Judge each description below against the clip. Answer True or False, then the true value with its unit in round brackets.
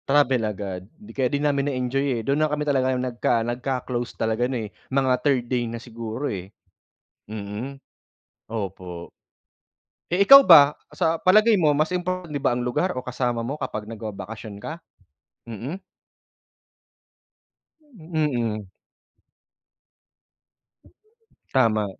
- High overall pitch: False (125 Hz)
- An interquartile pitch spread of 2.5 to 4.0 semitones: False (4.6 semitones)